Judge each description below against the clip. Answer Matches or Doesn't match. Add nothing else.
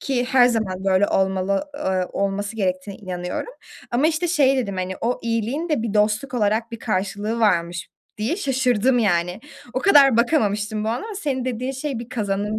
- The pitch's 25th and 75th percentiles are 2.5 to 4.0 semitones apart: Doesn't match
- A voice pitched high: Matches